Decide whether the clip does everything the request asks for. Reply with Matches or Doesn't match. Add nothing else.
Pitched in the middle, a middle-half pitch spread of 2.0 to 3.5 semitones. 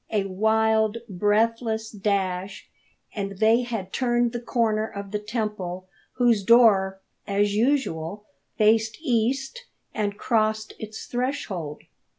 Doesn't match